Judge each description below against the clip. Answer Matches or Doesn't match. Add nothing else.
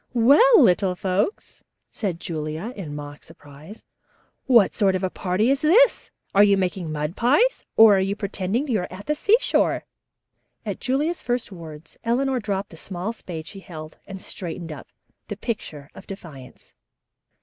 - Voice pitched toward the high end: Matches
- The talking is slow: Doesn't match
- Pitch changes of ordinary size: Doesn't match